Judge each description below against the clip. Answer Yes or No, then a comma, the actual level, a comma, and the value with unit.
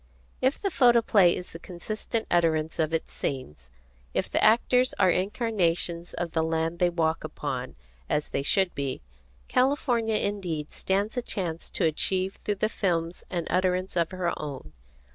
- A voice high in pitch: No, medium, 180 Hz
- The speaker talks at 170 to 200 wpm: No, average, 160 wpm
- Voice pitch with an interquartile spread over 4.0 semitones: Yes, average, 4.4 semitones